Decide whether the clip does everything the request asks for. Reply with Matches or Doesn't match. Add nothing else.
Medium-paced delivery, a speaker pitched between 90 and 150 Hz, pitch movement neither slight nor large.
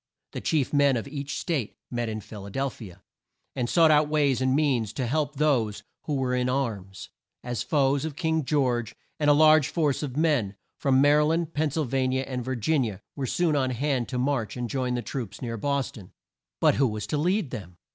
Doesn't match